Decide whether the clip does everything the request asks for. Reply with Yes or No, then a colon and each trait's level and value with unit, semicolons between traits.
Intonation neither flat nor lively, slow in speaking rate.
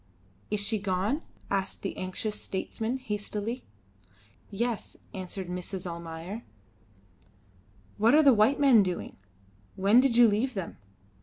Yes: average, 3.9 semitones; slow, 125 wpm